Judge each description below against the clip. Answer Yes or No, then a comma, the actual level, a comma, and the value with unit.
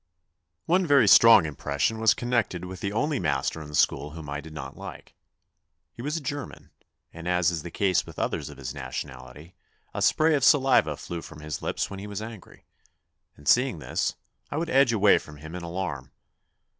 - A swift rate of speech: No, average, 195 wpm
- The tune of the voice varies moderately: No, wide, 7.9 semitones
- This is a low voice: Yes, very low, 90 Hz